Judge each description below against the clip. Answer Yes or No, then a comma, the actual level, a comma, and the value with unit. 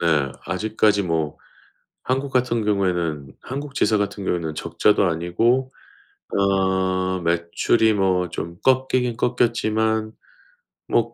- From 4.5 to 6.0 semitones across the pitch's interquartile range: Yes, average, 5.2 semitones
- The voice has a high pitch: No, low, 100 Hz